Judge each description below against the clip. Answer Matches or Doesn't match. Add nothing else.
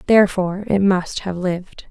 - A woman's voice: Matches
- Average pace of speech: Matches